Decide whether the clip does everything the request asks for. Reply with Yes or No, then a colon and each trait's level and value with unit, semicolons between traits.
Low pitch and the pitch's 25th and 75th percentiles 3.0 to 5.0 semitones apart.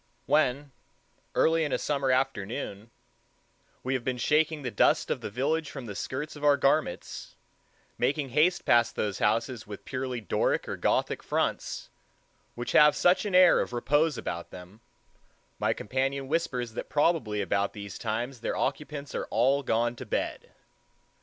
Yes: low, 130 Hz; average, 4.4 semitones